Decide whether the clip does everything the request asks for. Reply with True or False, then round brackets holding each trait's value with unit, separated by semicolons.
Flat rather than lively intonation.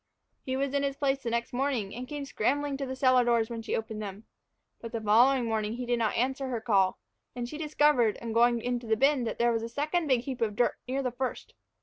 False (3.0 semitones)